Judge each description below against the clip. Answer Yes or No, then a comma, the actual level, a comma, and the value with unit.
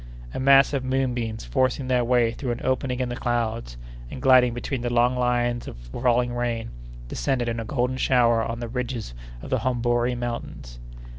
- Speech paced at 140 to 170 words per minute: No, average, 180 wpm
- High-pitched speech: No, low, 120 Hz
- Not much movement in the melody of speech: Yes, narrow, 1.4 semitones